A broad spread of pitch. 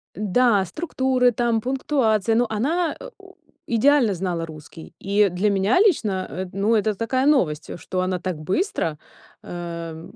Yes: wide, 5.8 semitones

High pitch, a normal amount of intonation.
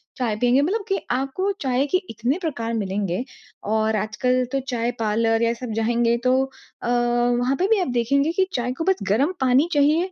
Yes: high, 245 Hz; average, 3.5 semitones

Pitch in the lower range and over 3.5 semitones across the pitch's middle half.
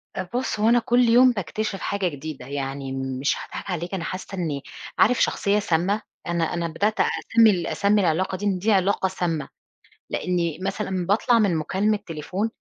No: medium, 185 Hz; average, 4.2 semitones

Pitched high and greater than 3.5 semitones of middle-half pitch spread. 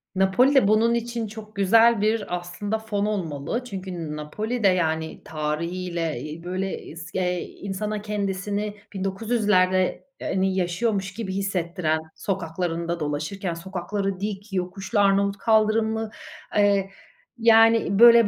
No: high, 195 Hz; average, 3.2 semitones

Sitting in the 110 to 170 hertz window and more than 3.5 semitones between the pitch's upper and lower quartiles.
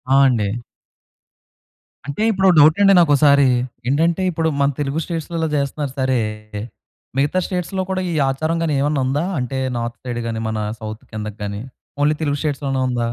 Yes: medium, 140 Hz; average, 4.5 semitones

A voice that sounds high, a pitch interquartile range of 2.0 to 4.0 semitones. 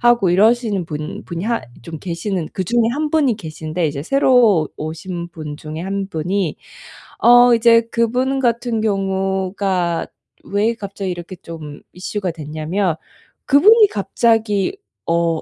No: high, 195 Hz; wide, 5.6 semitones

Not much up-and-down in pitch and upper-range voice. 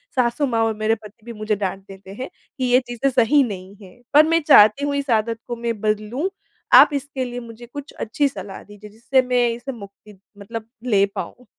No: average, 3.5 semitones; high, 230 Hz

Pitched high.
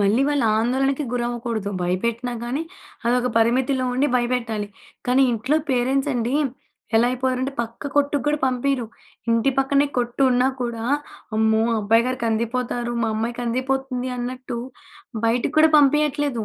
Yes: high, 245 Hz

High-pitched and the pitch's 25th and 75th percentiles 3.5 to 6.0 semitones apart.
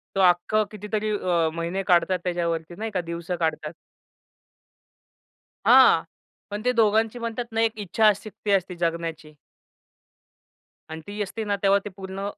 Yes: high, 195 Hz; average, 4.0 semitones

